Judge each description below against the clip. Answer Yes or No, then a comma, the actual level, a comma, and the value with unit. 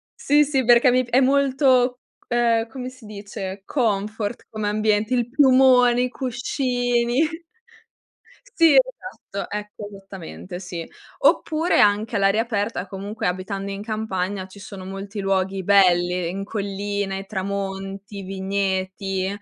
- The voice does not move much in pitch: No, average, 4.0 semitones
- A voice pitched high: Yes, high, 205 Hz